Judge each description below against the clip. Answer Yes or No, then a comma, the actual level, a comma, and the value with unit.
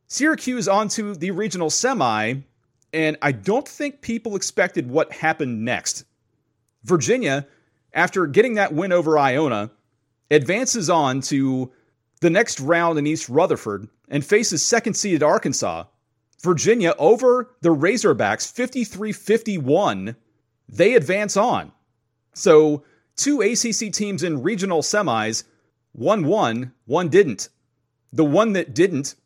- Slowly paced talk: Yes, slow, 120 wpm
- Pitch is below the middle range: No, medium, 155 Hz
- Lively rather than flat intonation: Yes, wide, 8.3 semitones